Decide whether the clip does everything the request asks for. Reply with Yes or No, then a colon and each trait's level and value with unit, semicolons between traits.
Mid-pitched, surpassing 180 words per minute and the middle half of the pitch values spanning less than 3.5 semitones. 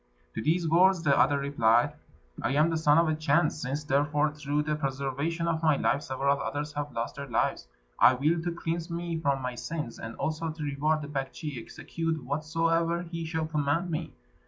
Yes: medium, 150 Hz; average, 195 wpm; average, 2.8 semitones